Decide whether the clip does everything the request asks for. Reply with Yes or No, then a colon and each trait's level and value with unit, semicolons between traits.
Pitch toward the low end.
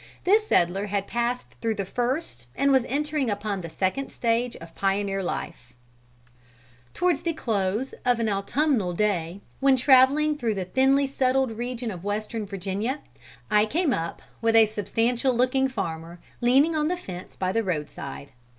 No: high, 225 Hz